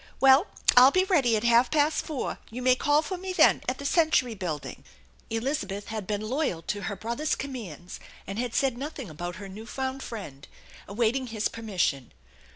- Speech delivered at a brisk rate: No, average, 180 wpm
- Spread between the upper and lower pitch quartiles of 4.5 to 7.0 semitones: Yes, average, 5.1 semitones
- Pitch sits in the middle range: No, high, 235 Hz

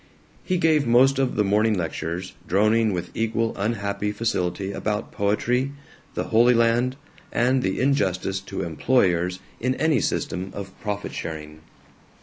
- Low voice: Yes, low, 105 Hz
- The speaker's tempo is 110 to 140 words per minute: Yes, slow, 135 wpm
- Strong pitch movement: No, average, 4.5 semitones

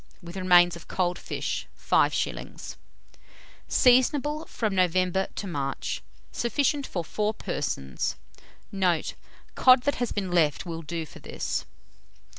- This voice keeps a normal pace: No, slow, 120 wpm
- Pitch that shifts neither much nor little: No, wide, 5.8 semitones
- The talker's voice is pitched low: No, medium, 185 Hz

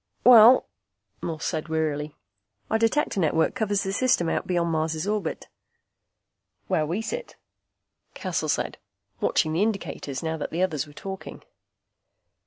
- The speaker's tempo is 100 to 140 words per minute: Yes, slow, 135 wpm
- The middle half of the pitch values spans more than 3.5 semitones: Yes, average, 5.2 semitones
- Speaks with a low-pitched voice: No, medium, 170 Hz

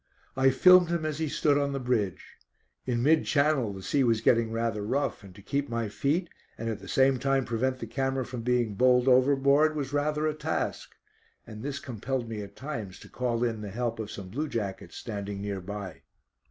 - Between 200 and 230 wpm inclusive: Yes, fast, 205 wpm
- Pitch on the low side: Yes, low, 125 Hz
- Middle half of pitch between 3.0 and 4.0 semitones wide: No, average, 4.4 semitones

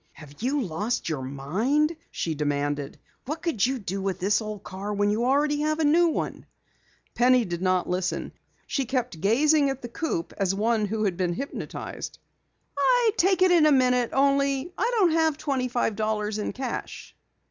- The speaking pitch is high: Yes, high, 240 Hz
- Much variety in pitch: Yes, wide, 7.2 semitones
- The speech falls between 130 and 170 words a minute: No, average, 180 wpm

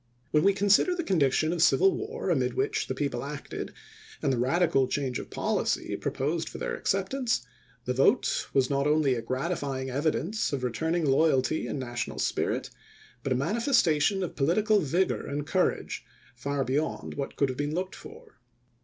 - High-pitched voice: No, medium, 155 Hz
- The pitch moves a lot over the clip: Yes, wide, 6.3 semitones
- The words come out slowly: No, average, 170 wpm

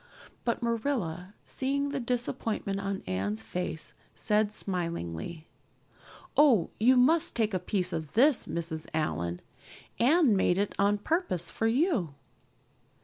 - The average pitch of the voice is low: No, high, 205 Hz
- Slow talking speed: Yes, slow, 125 wpm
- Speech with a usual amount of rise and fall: No, wide, 6.8 semitones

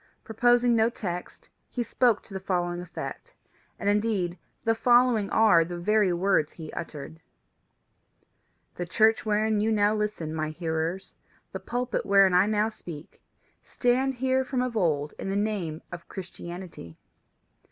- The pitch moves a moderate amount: Yes, average, 4.4 semitones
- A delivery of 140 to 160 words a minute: Yes, average, 150 wpm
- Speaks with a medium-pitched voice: No, high, 200 Hz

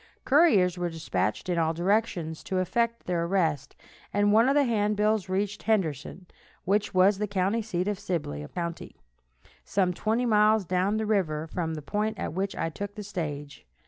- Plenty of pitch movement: No, average, 3.8 semitones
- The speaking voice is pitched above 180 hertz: Yes, high, 190 Hz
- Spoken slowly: No, average, 175 wpm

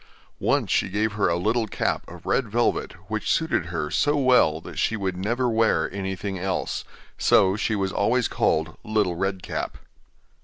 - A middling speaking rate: Yes, average, 170 wpm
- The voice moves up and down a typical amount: Yes, average, 3.4 semitones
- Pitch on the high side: No, low, 100 Hz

